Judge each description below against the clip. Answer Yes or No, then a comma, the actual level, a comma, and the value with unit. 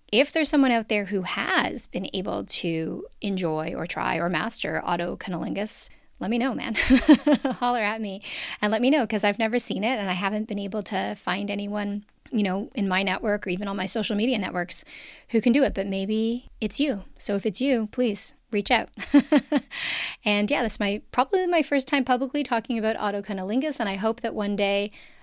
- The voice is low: No, high, 220 Hz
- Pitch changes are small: No, average, 4.2 semitones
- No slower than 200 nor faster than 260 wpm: Yes, fast, 205 wpm